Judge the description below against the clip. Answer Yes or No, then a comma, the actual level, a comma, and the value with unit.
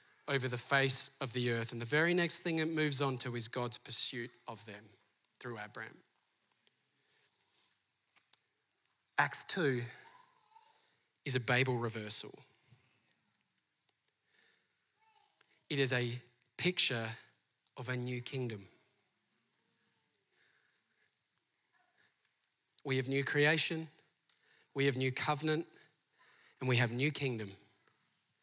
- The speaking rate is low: Yes, slow, 105 wpm